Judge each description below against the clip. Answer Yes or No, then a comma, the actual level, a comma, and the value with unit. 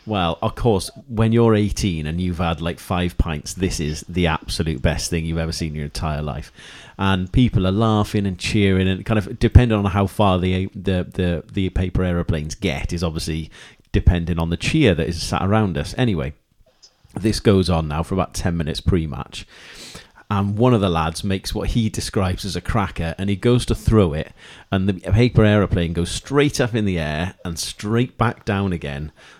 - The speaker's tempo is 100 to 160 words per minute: No, fast, 205 wpm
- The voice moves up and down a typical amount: Yes, average, 4.2 semitones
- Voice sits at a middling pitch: No, very low, 95 Hz